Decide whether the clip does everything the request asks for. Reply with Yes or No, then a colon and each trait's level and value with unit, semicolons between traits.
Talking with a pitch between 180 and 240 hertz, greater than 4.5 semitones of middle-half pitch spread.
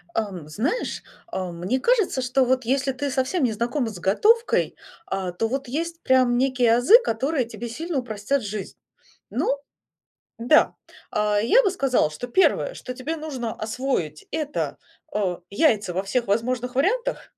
No: very high, 250 Hz; average, 4.9 semitones